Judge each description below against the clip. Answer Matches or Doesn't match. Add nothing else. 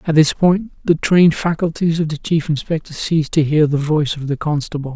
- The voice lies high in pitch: Doesn't match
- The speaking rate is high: Matches